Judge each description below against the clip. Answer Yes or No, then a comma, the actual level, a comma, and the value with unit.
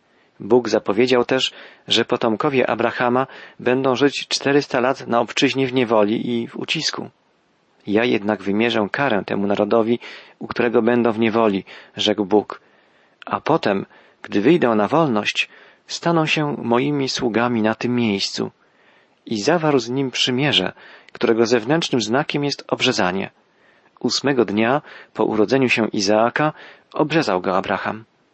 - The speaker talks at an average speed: Yes, average, 130 wpm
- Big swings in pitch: No, average, 3.3 semitones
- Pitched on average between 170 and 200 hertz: No, low, 120 Hz